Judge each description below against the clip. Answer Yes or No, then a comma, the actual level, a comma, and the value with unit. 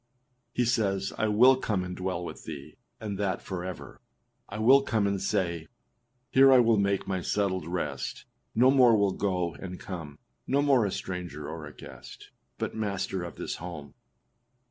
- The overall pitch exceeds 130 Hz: No, low, 100 Hz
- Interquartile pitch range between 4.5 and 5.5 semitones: No, average, 3.6 semitones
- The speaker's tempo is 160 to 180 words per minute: Yes, average, 170 wpm